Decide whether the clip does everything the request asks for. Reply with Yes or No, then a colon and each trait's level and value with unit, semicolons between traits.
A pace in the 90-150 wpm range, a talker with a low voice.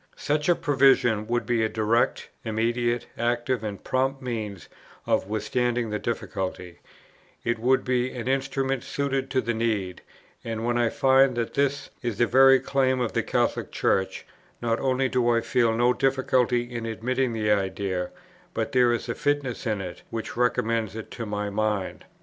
No: average, 170 wpm; low, 120 Hz